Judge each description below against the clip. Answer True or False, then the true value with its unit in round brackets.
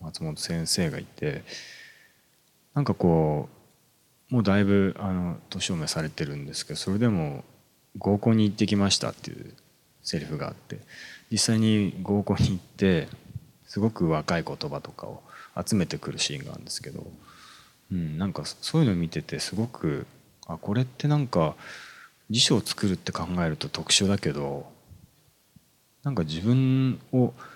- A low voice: True (100 Hz)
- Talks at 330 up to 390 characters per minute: False (305 characters per minute)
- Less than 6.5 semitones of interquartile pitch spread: True (5.1 semitones)